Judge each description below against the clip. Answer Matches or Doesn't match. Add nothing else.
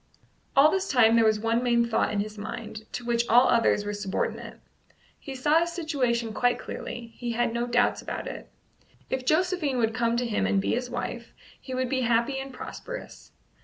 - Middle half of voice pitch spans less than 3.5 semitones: Matches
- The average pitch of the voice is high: Matches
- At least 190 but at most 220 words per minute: Matches